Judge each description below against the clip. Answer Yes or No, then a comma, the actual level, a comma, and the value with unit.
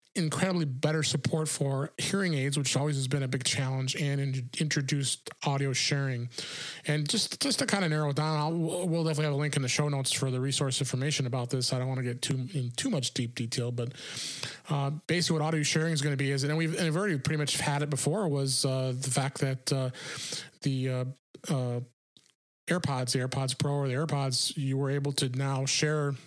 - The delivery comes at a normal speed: No, fast, 220 wpm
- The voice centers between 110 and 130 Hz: No, medium, 140 Hz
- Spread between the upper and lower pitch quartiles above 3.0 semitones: No, narrow, 2.6 semitones